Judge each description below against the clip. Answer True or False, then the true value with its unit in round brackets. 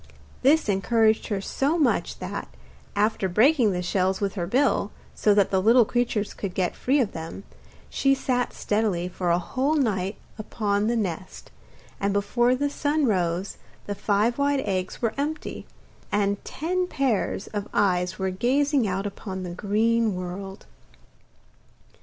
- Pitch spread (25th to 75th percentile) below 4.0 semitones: False (4.7 semitones)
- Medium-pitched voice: False (210 Hz)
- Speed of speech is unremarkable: True (155 wpm)